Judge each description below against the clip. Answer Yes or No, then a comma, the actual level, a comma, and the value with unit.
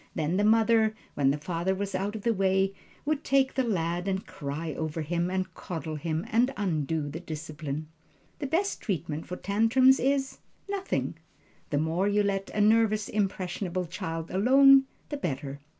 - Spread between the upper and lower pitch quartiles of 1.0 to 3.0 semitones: No, wide, 5.6 semitones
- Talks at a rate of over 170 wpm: No, average, 165 wpm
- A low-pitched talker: No, high, 190 Hz